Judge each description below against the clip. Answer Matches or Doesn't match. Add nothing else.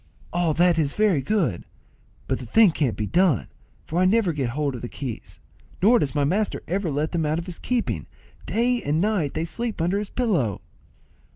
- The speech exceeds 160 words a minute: Matches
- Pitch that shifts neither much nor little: Doesn't match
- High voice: Doesn't match